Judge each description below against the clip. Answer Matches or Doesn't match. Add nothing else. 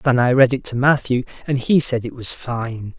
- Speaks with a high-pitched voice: Doesn't match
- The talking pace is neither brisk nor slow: Doesn't match